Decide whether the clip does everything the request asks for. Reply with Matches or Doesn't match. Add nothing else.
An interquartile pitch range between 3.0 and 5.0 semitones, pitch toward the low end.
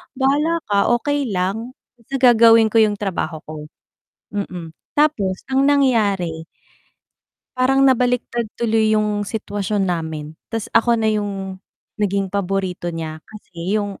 Doesn't match